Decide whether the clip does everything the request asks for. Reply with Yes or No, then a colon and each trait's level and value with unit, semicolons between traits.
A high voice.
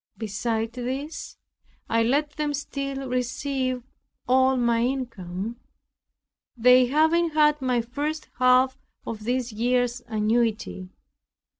Yes: very high, 250 Hz